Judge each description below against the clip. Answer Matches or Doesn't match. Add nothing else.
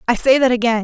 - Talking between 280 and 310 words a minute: Matches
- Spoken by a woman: Matches